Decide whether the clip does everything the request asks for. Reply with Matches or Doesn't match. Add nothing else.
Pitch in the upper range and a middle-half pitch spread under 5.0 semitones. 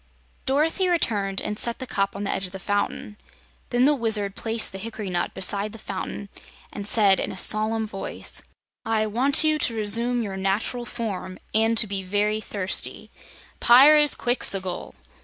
Matches